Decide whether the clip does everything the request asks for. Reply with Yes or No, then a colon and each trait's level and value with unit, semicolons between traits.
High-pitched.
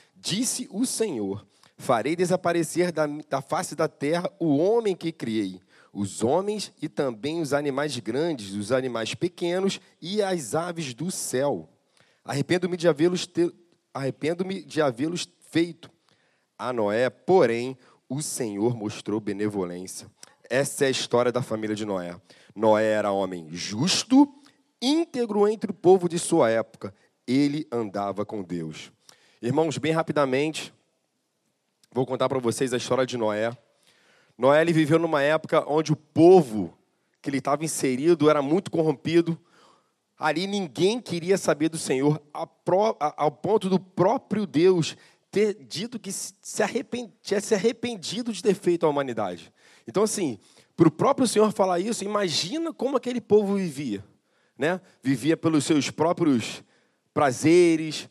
No: medium, 160 Hz